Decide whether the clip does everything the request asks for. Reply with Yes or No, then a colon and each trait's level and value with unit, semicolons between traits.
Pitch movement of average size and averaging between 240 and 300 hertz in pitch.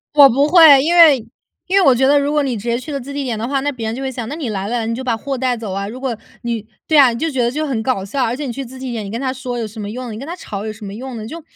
Yes: average, 3.6 semitones; very high, 255 Hz